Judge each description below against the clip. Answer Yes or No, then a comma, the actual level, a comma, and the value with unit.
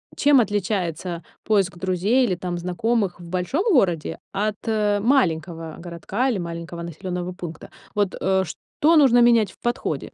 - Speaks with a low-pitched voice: No, high, 190 Hz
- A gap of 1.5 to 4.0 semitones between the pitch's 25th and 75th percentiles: No, average, 4.4 semitones